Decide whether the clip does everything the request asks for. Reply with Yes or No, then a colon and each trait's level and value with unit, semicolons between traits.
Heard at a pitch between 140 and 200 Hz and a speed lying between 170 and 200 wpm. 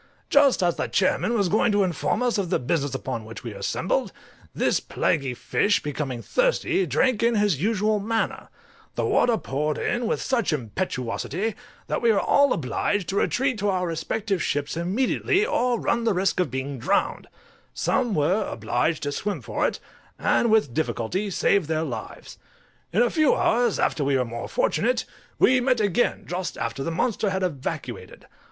Yes: high, 190 Hz; average, 175 wpm